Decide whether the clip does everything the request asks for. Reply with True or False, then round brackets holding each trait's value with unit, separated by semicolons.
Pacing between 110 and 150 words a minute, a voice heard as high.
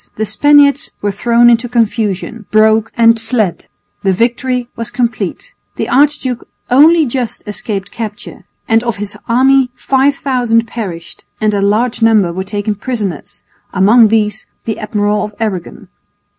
True (140 wpm; 225 Hz)